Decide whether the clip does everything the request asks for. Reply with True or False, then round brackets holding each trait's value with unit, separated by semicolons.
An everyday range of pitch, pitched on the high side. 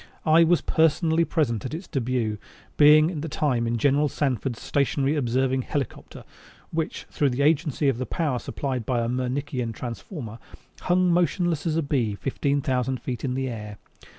False (4.0 semitones; 135 Hz)